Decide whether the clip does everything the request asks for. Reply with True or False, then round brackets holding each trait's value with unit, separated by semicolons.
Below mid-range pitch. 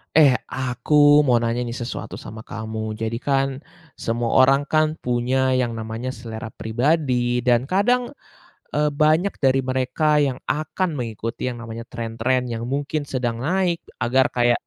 True (130 Hz)